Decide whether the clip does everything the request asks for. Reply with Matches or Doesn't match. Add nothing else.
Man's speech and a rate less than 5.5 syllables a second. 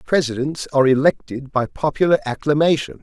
Doesn't match